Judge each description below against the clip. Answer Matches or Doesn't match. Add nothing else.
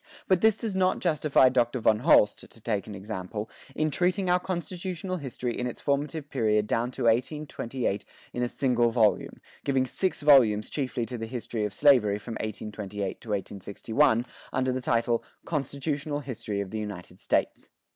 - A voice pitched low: Matches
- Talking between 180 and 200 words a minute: Doesn't match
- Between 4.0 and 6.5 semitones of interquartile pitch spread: Matches